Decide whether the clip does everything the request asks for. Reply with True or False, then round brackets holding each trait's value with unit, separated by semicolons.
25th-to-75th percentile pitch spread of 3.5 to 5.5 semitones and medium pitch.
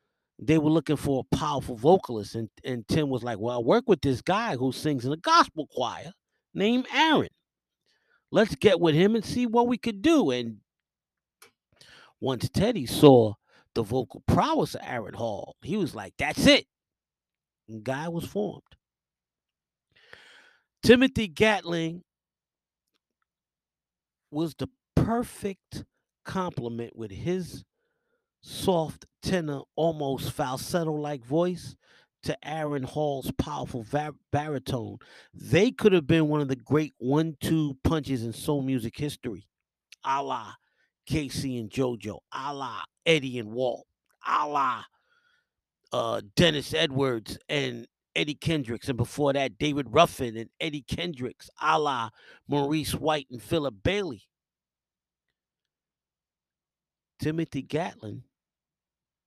True (4.9 semitones; 145 Hz)